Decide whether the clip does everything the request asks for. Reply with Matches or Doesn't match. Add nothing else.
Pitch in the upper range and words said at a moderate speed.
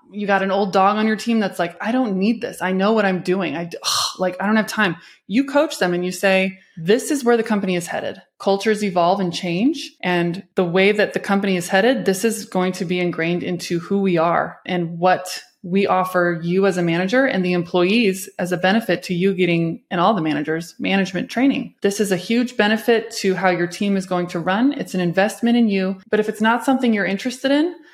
Doesn't match